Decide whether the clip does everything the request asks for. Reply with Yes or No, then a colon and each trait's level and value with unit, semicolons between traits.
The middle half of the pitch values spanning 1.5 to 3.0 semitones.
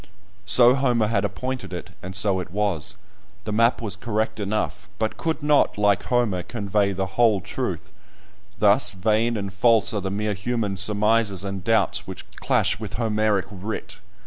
Yes: narrow, 2.6 semitones